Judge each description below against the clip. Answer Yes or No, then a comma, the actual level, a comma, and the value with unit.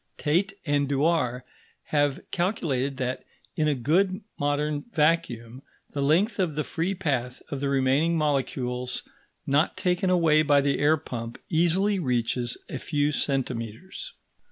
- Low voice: No, medium, 145 Hz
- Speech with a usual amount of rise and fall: Yes, average, 4.2 semitones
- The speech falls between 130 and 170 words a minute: Yes, slow, 135 wpm